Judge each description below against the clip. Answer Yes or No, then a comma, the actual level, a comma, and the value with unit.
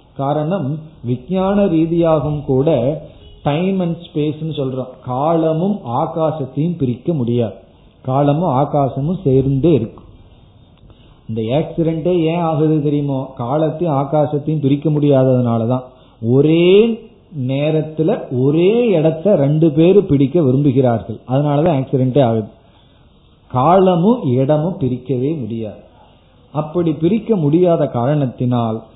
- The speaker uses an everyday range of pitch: Yes, average, 4.1 semitones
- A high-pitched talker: No, medium, 145 Hz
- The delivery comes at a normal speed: Yes, average, 85 wpm